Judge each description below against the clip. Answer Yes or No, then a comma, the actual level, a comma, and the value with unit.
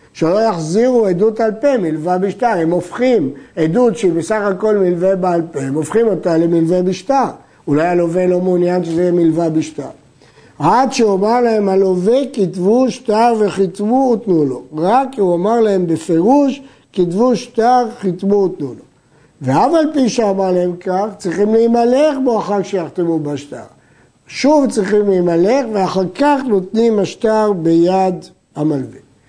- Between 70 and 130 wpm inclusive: No, average, 145 wpm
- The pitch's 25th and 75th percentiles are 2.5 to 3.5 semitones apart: No, average, 4.8 semitones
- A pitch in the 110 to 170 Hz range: No, high, 195 Hz